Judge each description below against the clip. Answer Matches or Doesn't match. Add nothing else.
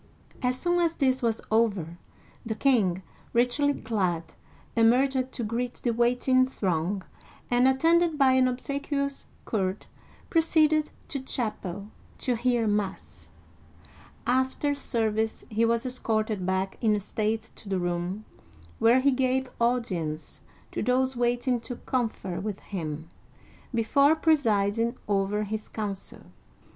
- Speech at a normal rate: Doesn't match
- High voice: Matches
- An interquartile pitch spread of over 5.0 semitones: Doesn't match